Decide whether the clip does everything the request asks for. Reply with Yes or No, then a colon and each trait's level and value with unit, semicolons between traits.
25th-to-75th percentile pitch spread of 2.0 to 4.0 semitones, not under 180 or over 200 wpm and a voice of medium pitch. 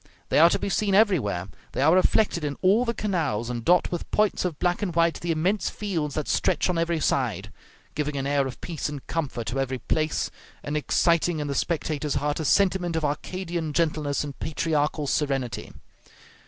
Yes: average, 3.6 semitones; average, 195 wpm; medium, 155 Hz